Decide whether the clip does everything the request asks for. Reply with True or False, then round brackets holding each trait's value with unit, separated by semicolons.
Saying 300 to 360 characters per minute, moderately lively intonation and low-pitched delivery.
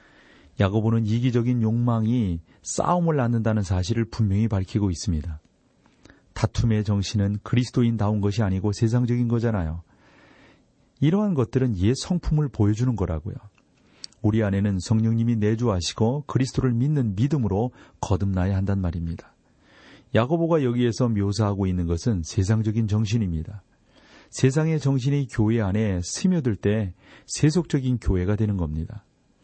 True (330 characters per minute; 3.7 semitones; 110 Hz)